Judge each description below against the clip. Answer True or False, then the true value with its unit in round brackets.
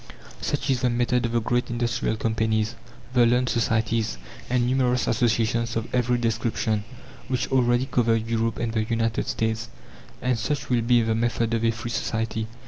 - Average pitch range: False (1.6 semitones)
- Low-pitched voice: True (115 Hz)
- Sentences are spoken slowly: False (170 wpm)